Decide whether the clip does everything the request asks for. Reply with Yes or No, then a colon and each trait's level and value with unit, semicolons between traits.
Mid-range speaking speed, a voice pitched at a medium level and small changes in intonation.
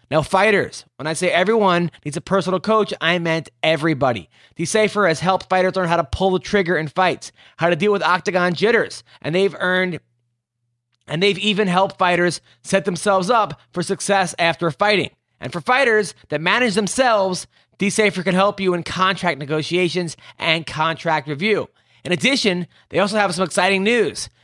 No: average, 170 wpm; medium, 180 Hz; average, 3.5 semitones